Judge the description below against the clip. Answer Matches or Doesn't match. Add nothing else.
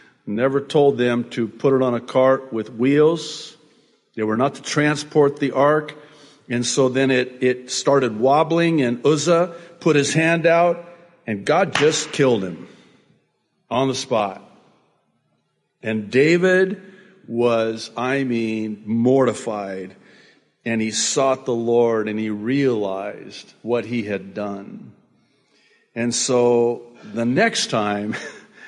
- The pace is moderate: Doesn't match